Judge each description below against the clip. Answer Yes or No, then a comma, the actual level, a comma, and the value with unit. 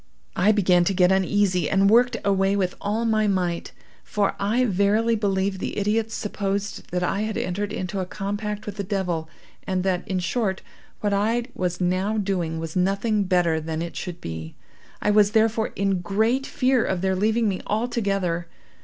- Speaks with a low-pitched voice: No, high, 195 Hz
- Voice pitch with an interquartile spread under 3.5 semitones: Yes, average, 2.7 semitones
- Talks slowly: No, average, 180 wpm